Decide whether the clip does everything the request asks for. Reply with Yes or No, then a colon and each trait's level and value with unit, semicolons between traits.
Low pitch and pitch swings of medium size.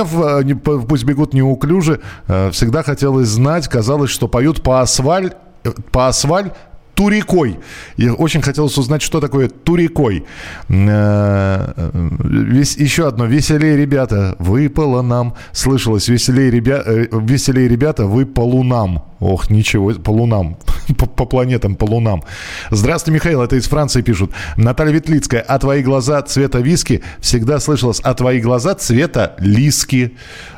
Yes: low, 130 Hz; average, 4.1 semitones